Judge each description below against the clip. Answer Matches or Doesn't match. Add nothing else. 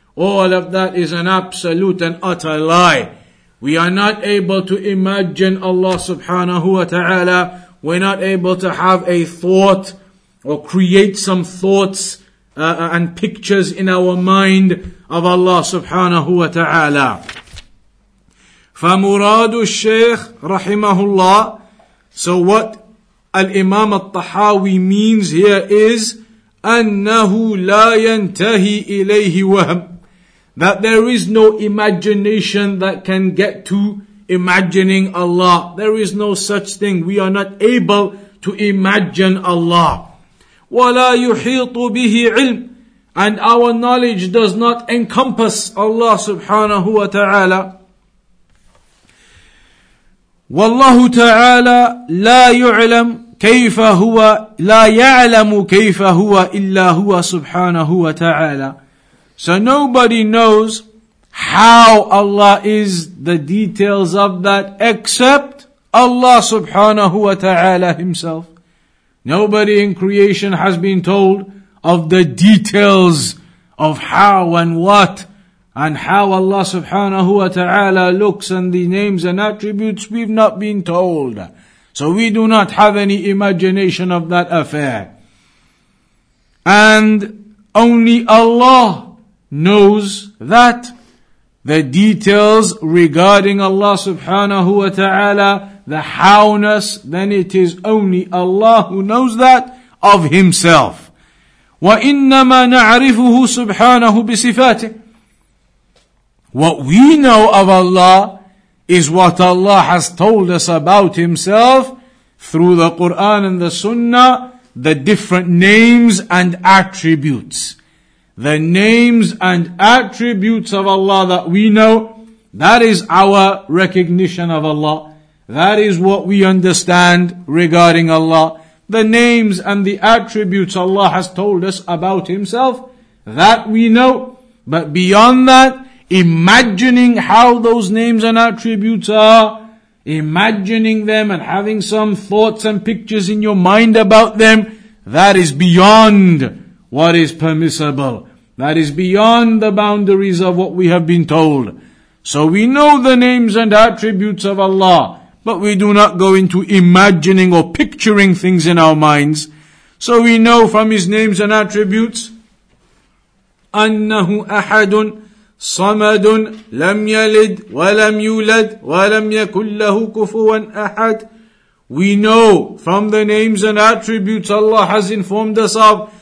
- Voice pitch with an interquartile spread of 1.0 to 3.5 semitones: Matches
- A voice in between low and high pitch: Doesn't match